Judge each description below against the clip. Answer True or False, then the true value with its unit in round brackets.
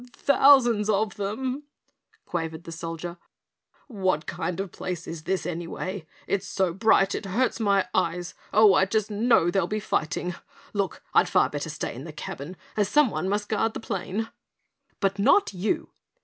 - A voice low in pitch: False (195 Hz)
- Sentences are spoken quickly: False (165 wpm)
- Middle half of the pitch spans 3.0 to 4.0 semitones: True (3.5 semitones)